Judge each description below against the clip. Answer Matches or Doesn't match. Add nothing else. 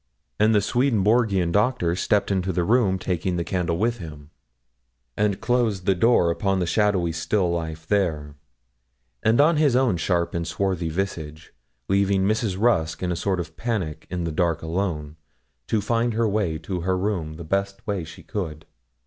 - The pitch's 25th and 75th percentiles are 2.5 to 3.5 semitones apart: Doesn't match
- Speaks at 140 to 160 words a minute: Doesn't match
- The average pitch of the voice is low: Matches